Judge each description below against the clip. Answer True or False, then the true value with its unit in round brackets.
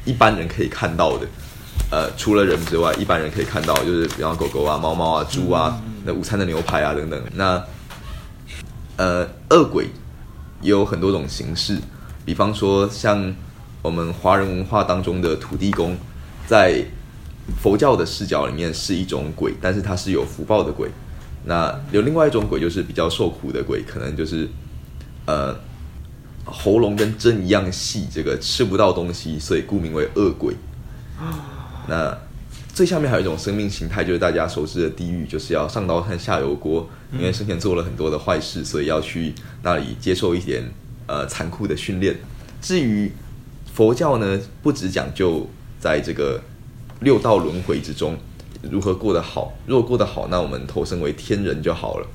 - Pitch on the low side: True (95 Hz)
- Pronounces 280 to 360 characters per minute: False (260 characters per minute)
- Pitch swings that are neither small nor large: True (4.4 semitones)